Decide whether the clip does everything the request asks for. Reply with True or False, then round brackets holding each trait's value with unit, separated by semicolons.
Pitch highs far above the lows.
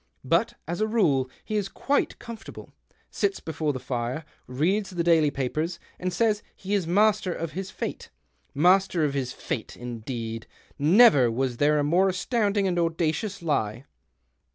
True (6.2 semitones)